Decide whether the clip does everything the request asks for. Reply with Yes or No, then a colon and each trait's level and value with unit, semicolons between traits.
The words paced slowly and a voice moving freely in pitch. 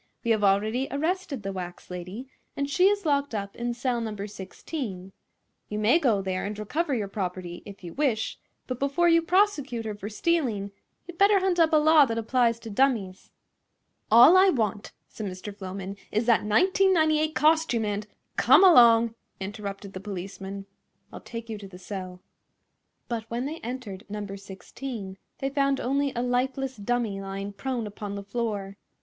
No: average, 170 wpm; wide, 5.7 semitones